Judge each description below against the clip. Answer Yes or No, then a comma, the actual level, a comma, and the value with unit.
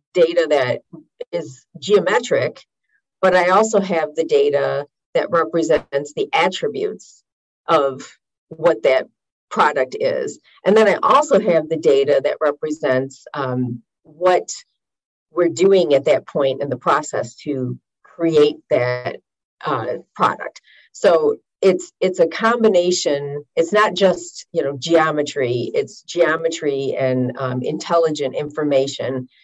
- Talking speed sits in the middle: No, slow, 120 wpm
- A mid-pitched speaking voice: Yes, medium, 170 Hz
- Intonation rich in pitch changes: Yes, wide, 7.0 semitones